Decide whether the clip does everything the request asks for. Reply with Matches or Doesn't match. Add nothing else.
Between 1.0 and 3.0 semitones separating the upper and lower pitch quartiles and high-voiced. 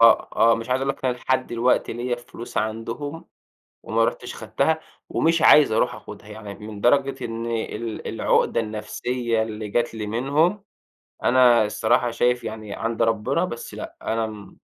Doesn't match